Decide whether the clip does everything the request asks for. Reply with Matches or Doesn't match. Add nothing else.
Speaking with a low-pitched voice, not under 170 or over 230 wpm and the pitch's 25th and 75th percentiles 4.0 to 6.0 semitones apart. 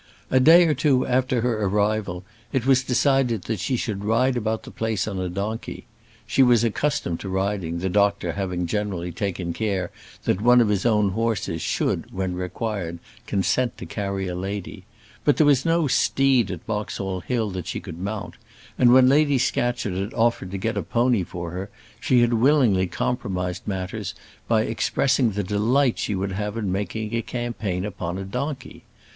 Matches